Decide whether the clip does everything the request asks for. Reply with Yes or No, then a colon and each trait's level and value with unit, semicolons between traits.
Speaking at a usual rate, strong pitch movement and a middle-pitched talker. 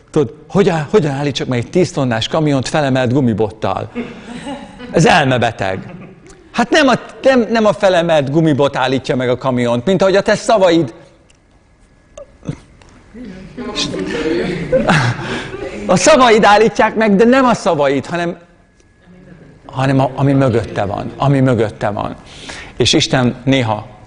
Yes: average, 125 wpm; wide, 7.3 semitones; medium, 150 Hz